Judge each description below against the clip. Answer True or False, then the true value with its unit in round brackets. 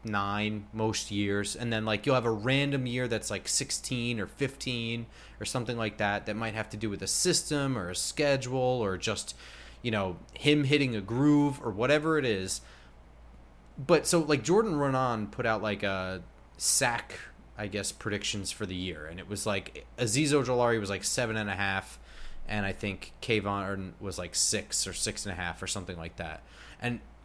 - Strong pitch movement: False (4.5 semitones)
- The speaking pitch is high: False (105 Hz)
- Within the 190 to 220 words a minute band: True (195 wpm)